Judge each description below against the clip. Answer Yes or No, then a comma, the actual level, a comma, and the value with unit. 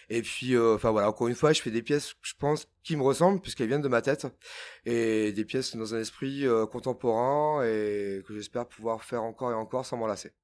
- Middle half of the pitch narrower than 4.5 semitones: Yes, average, 3.4 semitones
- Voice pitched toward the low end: Yes, low, 120 Hz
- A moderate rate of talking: No, fast, 230 wpm